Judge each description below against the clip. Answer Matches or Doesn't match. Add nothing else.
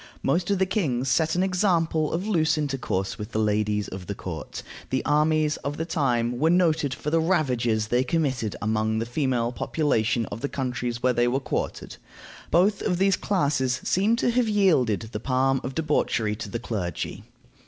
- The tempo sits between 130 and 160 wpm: Doesn't match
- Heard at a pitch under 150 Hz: Matches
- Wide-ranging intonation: Matches